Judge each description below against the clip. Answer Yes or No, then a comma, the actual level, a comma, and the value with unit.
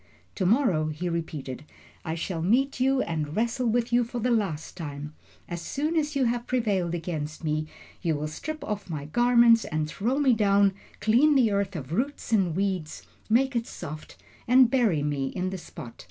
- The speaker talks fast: No, average, 185 wpm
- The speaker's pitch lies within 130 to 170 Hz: No, high, 200 Hz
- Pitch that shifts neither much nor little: No, wide, 7.3 semitones